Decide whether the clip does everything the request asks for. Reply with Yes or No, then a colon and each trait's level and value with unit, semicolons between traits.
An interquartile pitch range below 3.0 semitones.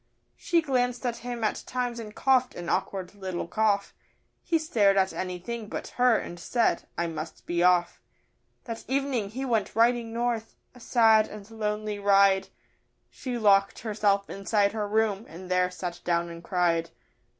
No: average, 4.0 semitones